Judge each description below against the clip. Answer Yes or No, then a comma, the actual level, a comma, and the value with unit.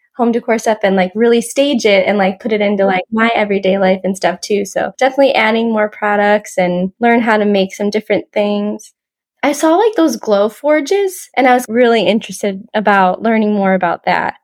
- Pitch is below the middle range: No, high, 215 Hz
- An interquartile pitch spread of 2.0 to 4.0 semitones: Yes, average, 3.2 semitones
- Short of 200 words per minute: No, fast, 205 wpm